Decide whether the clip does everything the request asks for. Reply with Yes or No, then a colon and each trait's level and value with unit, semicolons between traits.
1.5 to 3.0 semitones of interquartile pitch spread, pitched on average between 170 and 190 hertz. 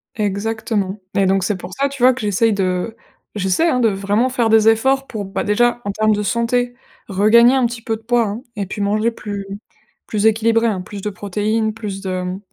No: narrow, 2.6 semitones; high, 215 Hz